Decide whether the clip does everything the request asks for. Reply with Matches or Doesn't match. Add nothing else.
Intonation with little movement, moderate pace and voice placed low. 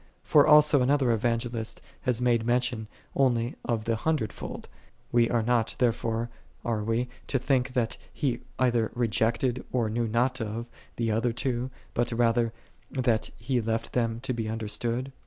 Matches